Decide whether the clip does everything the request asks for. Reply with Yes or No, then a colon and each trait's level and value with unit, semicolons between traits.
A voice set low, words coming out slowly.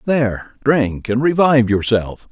Yes: low, 120 Hz; slow, 130 wpm